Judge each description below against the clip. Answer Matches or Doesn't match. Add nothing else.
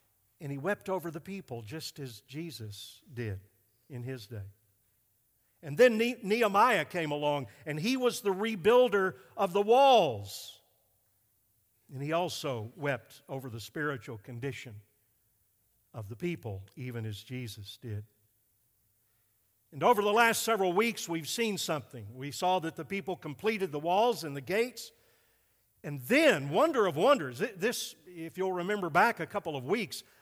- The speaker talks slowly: Doesn't match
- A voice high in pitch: Doesn't match